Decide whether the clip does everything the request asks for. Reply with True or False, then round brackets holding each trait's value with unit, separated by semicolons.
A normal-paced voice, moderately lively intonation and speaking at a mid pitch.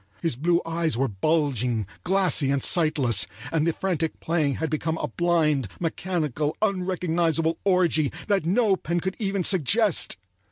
True (145 wpm; 3.3 semitones; 165 Hz)